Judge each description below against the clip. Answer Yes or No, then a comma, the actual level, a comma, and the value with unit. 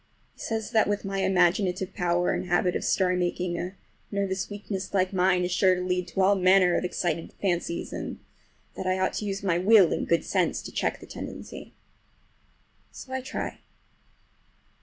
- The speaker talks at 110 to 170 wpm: No, average, 180 wpm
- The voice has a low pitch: No, medium, 185 Hz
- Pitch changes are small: Yes, narrow, 1.7 semitones